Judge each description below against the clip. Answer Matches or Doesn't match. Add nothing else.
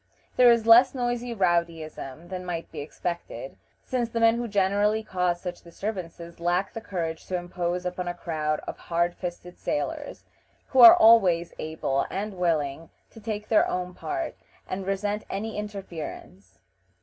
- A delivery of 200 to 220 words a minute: Doesn't match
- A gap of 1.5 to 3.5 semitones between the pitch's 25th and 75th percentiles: Doesn't match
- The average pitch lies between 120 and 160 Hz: Doesn't match